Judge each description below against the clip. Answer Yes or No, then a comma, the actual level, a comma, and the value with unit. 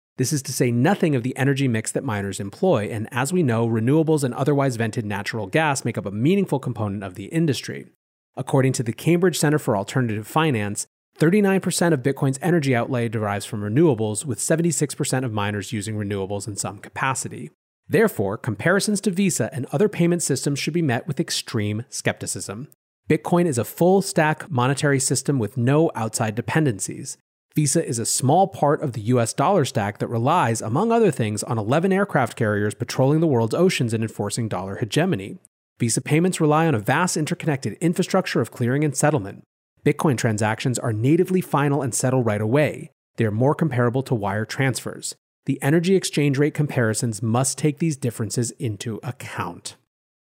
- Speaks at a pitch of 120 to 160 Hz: Yes, low, 135 Hz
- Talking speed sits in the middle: Yes, average, 175 wpm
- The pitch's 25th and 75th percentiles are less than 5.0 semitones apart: No, wide, 5.4 semitones